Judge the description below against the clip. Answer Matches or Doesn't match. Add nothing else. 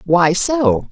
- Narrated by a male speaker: Doesn't match